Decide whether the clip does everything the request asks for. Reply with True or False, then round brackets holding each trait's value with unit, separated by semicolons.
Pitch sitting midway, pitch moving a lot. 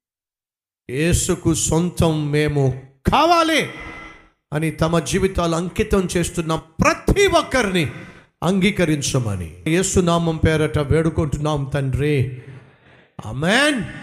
False (160 Hz; 4.5 semitones)